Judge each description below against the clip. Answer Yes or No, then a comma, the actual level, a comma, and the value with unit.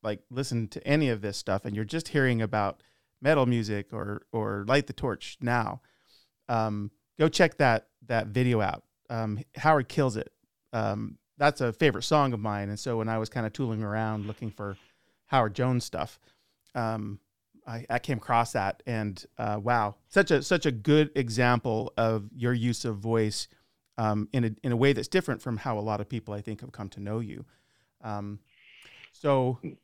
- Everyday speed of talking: Yes, average, 190 wpm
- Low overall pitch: Yes, low, 115 Hz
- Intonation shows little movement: No, average, 3.8 semitones